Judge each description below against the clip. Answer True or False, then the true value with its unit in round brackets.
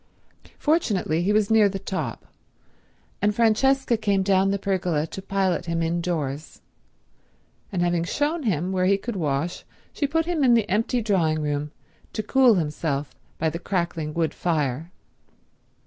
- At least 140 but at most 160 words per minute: True (150 wpm)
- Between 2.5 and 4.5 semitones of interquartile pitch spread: False (4.9 semitones)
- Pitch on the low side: False (185 Hz)